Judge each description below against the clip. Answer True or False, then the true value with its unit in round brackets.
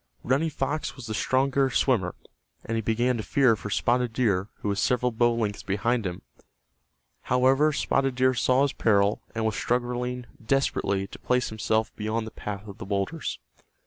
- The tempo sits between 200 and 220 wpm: False (175 wpm)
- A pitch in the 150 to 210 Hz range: False (120 Hz)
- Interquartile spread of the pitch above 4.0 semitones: False (3.5 semitones)